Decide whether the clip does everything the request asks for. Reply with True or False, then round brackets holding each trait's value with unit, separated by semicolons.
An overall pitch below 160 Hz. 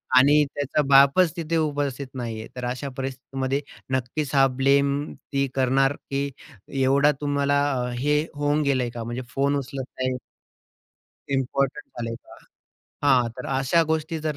True (140 Hz)